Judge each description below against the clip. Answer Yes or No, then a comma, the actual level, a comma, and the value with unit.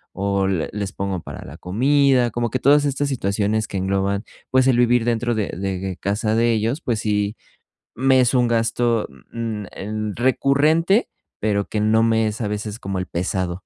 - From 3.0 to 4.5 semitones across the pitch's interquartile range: Yes, average, 3.7 semitones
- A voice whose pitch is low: Yes, low, 110 Hz